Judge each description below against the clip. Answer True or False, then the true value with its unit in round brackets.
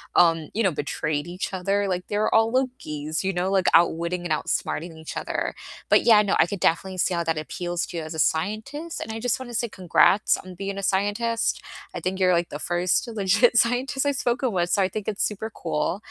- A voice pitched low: False (190 Hz)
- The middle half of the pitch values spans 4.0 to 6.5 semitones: True (4.3 semitones)